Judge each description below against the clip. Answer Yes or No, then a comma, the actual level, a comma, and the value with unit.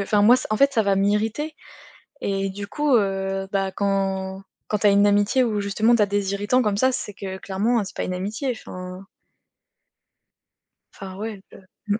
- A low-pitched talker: No, high, 205 Hz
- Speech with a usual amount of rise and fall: No, narrow, 2.1 semitones